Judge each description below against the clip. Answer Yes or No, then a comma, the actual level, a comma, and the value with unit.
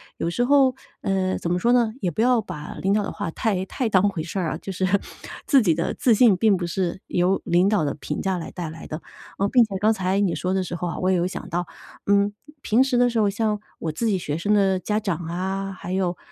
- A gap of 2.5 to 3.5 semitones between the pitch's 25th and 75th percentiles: Yes, average, 3.2 semitones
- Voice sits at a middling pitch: No, high, 195 Hz